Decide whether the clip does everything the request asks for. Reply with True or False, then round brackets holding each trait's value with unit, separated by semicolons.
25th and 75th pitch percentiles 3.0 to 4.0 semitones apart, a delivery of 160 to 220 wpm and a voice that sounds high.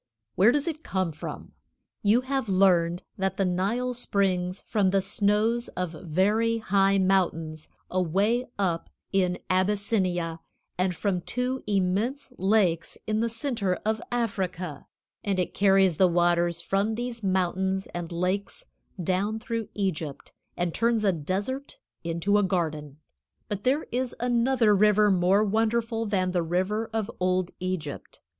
False (3.5 semitones; 140 wpm; 195 Hz)